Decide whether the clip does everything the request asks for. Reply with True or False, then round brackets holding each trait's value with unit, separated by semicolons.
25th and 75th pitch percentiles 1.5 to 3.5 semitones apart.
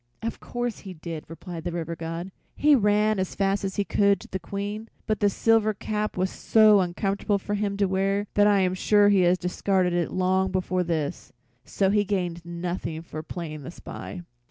True (2.8 semitones)